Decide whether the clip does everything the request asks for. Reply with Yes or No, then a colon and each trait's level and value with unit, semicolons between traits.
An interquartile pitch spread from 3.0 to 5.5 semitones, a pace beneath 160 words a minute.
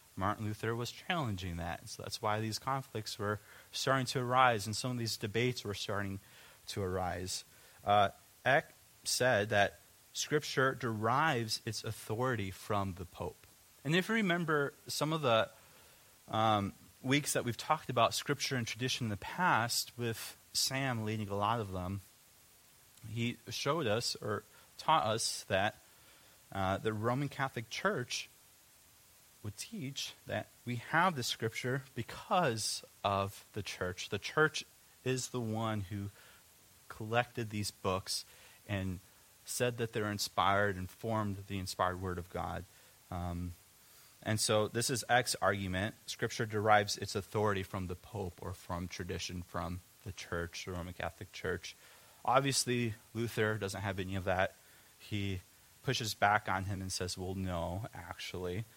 Yes: average, 3.9 semitones; average, 150 wpm